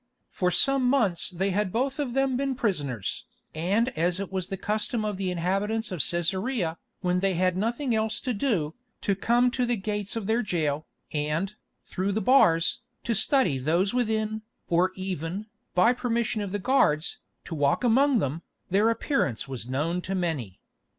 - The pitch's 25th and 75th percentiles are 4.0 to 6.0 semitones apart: Yes, average, 5.2 semitones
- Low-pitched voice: No, high, 195 Hz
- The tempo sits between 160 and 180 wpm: Yes, average, 175 wpm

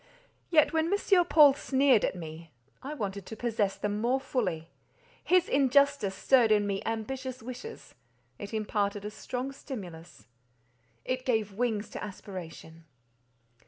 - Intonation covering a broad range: Yes, wide, 6.9 semitones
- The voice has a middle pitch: No, high, 215 Hz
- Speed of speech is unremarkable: No, slow, 125 wpm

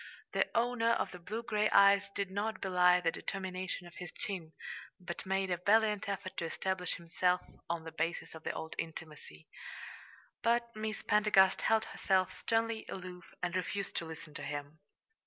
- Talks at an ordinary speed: Yes, average, 170 wpm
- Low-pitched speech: No, medium, 185 Hz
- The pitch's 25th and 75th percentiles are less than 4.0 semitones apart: Yes, average, 3.5 semitones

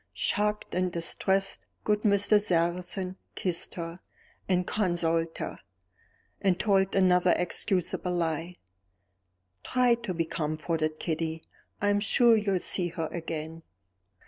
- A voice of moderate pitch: Yes, medium, 180 Hz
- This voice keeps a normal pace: No, slow, 120 wpm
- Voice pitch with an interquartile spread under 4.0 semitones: Yes, average, 3.2 semitones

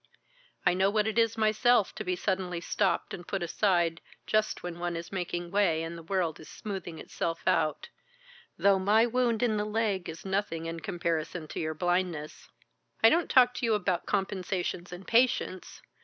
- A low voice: No, medium, 185 Hz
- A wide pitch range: No, average, 3.8 semitones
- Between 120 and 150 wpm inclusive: No, average, 180 wpm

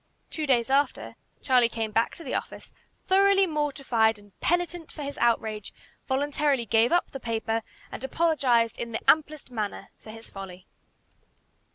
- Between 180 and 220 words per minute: No, average, 155 wpm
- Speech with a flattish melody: No, average, 5.1 semitones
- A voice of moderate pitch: No, very high, 250 Hz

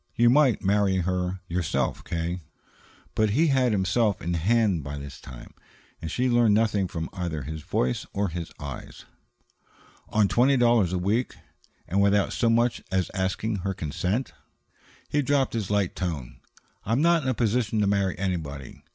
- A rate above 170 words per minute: No, average, 165 wpm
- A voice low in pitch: Yes, low, 100 Hz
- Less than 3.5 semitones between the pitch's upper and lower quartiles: No, average, 5.0 semitones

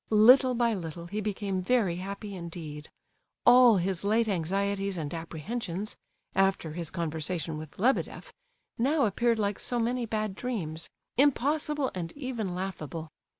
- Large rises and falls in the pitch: Yes, wide, 5.7 semitones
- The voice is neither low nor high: No, high, 200 Hz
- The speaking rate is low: Yes, slow, 130 wpm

